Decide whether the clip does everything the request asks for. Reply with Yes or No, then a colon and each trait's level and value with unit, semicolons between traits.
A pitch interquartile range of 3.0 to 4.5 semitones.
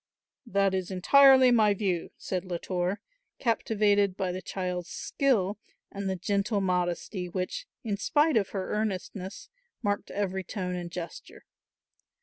No: narrow, 2.6 semitones